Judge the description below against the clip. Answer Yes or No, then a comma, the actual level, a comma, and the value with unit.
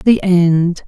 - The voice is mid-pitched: Yes, medium, 180 Hz